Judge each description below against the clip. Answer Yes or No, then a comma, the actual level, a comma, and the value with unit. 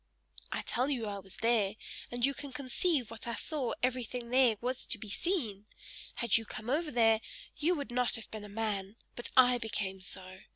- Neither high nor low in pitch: No, high, 235 Hz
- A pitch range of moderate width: Yes, average, 3.3 semitones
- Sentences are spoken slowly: No, average, 200 wpm